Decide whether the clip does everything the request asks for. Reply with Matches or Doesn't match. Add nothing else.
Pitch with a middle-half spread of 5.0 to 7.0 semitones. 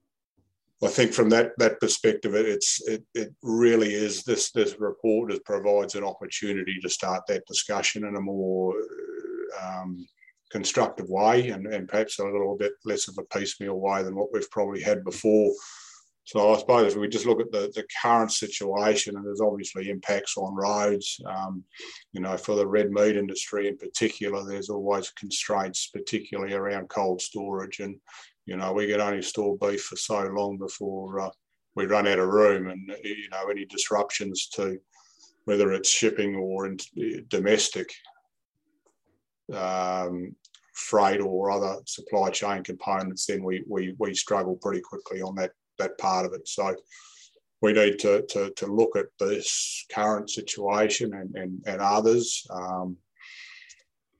Doesn't match